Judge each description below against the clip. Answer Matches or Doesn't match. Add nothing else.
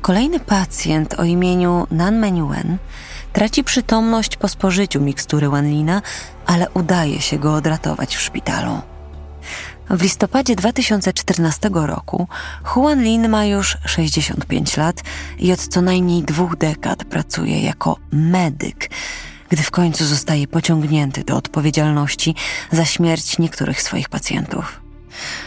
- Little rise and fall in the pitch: Doesn't match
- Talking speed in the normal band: Matches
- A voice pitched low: Doesn't match